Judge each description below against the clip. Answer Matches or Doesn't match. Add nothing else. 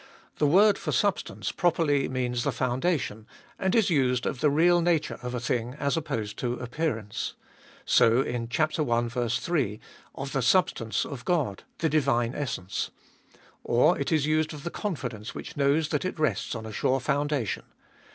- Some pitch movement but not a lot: Matches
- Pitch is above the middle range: Doesn't match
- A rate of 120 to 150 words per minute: Doesn't match